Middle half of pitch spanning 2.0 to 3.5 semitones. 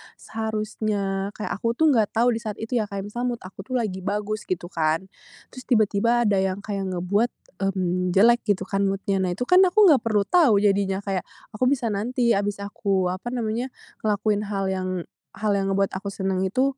Yes: average, 3.0 semitones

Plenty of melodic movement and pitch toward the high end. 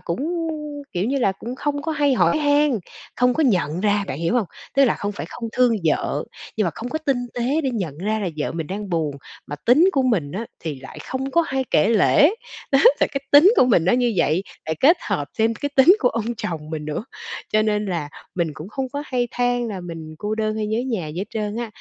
Yes: wide, 6.9 semitones; high, 220 Hz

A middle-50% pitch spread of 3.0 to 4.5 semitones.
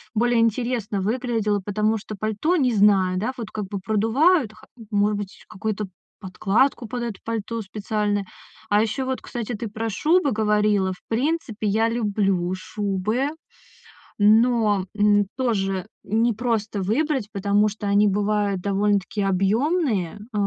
No: narrow, 2.4 semitones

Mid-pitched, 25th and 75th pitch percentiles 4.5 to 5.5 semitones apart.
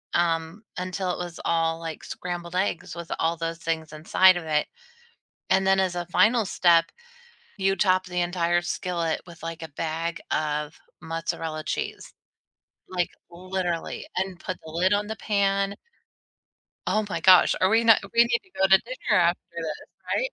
No: medium, 175 Hz; narrow, 2.6 semitones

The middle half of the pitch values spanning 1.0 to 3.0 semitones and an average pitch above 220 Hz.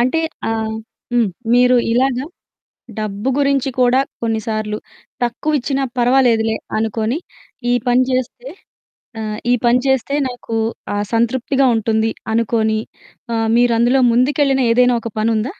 Yes: narrow, 2.6 semitones; high, 240 Hz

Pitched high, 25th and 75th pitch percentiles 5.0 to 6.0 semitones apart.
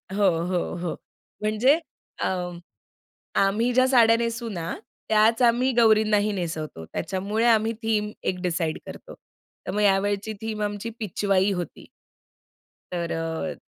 No: high, 210 Hz; average, 3.3 semitones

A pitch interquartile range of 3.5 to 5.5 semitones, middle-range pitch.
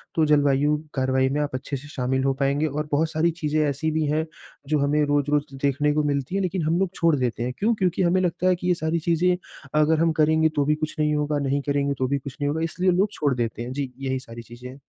No: average, 2.7 semitones; medium, 150 Hz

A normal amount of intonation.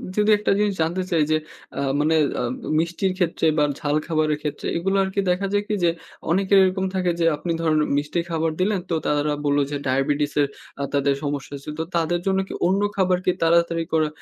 Yes: average, 4.1 semitones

